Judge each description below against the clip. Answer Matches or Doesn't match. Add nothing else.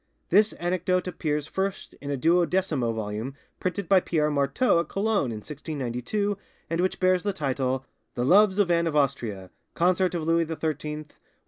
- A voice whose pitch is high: Doesn't match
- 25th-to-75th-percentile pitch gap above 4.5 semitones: Matches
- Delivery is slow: Doesn't match